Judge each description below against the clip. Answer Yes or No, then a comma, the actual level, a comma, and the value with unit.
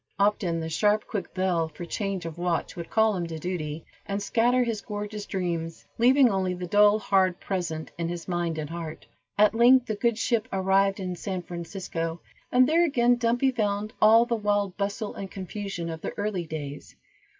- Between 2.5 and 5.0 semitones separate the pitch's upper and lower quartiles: Yes, average, 3.9 semitones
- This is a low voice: No, high, 195 Hz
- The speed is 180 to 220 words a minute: Yes, average, 185 wpm